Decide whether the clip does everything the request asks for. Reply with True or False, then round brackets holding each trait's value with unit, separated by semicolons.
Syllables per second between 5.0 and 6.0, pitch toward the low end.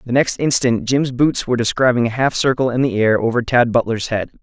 True (5.7 syllables/s; 120 Hz)